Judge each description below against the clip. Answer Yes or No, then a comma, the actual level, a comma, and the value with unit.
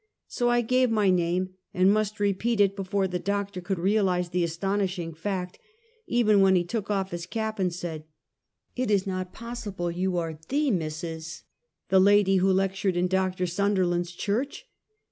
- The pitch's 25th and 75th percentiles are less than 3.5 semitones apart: Yes, narrow, 2.5 semitones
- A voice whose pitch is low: No, high, 190 Hz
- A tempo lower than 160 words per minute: No, average, 170 wpm